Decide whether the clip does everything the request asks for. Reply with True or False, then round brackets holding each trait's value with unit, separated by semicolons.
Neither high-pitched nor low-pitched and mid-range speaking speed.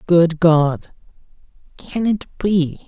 False (170 Hz; 105 wpm)